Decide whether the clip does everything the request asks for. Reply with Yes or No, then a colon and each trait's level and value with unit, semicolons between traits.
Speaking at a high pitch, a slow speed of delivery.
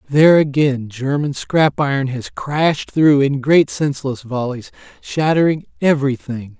No: medium, 140 Hz; slow, 125 wpm